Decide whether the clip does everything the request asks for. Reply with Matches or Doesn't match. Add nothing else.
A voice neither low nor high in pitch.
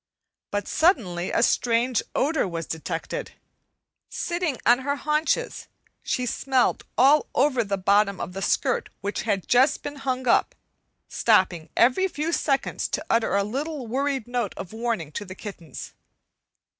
Doesn't match